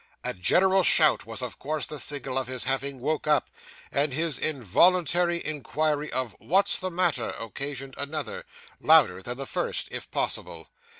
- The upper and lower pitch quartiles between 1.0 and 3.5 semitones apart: No, average, 4.4 semitones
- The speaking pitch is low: No, medium, 145 Hz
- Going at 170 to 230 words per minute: No, average, 160 wpm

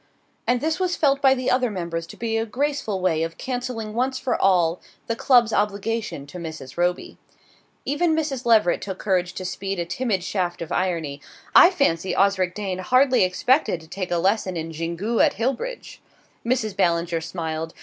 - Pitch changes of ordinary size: No, wide, 6.4 semitones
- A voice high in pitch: Yes, high, 195 Hz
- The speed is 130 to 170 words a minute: No, average, 180 wpm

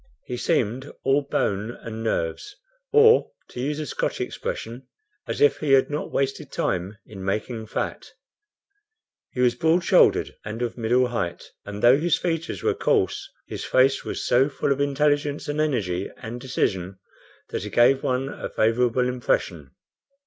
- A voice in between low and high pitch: No, low, 125 Hz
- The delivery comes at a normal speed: Yes, average, 160 wpm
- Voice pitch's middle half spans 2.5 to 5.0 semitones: Yes, average, 4.3 semitones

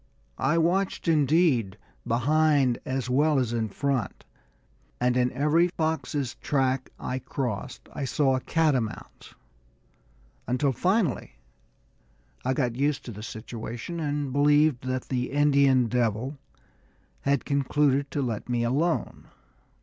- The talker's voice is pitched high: No, low, 135 Hz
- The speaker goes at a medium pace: No, slow, 120 wpm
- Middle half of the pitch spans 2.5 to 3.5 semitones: Yes, average, 3.2 semitones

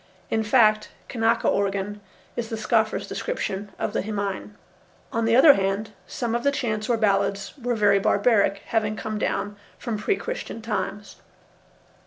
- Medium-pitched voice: No, high, 215 Hz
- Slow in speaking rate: No, average, 155 wpm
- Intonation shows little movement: Yes, narrow, 2.2 semitones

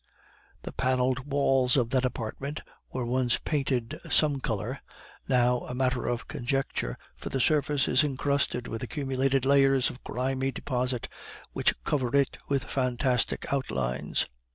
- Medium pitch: No, low, 130 Hz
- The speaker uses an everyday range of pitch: No, narrow, 1.8 semitones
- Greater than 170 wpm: No, slow, 135 wpm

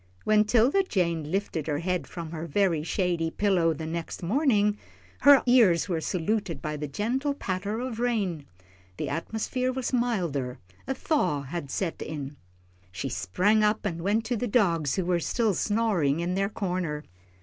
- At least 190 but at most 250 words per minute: No, average, 165 wpm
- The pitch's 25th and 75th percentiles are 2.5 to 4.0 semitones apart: No, average, 5.3 semitones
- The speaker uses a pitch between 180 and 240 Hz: Yes, medium, 185 Hz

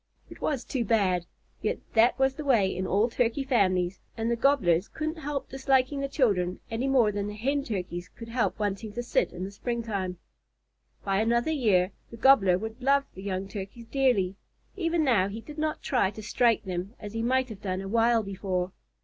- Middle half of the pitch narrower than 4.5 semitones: No, average, 5.1 semitones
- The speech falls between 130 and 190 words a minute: No, average, 200 wpm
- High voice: Yes, high, 225 Hz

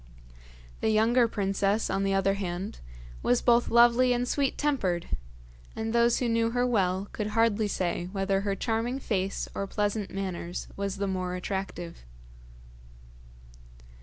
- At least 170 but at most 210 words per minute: No, average, 140 wpm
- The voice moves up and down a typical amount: Yes, average, 3.3 semitones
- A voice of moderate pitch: No, high, 205 Hz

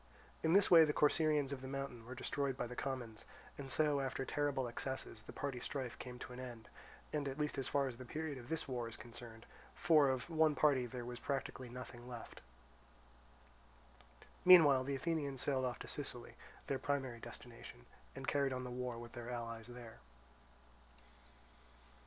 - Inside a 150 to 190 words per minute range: Yes, average, 175 wpm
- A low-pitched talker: Yes, low, 130 Hz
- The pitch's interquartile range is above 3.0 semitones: No, average, 2.7 semitones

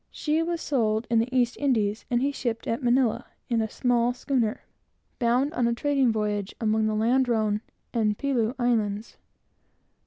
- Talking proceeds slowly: No, average, 160 wpm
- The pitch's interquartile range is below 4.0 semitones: Yes, average, 3.0 semitones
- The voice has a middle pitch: No, high, 235 Hz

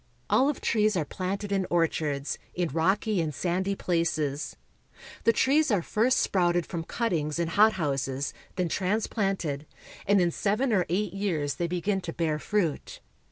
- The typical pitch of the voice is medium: Yes, medium, 180 Hz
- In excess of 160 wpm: No, average, 155 wpm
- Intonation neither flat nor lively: Yes, average, 4.2 semitones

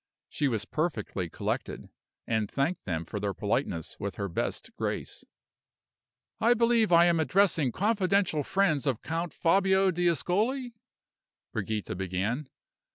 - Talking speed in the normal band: No, slow, 125 wpm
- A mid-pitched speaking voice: Yes, medium, 160 Hz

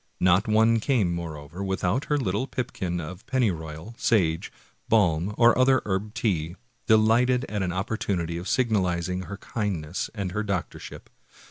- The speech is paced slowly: No, average, 145 wpm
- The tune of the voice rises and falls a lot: No, average, 4.5 semitones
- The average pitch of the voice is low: Yes, low, 100 Hz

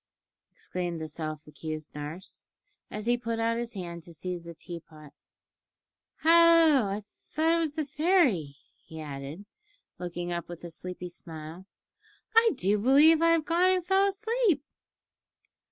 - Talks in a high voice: Yes, high, 200 Hz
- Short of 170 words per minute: Yes, average, 150 wpm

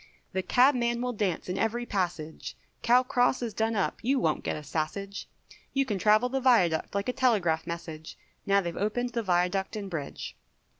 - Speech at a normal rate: Yes, average, 185 wpm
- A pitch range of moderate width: No, wide, 5.7 semitones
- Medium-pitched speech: No, high, 205 Hz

